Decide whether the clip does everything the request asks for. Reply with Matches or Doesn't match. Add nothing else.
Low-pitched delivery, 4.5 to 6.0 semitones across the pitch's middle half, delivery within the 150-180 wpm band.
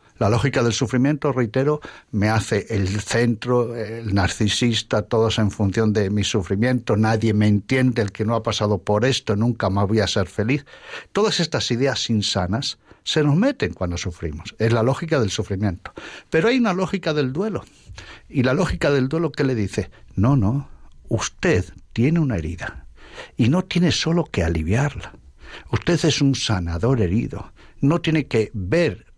Matches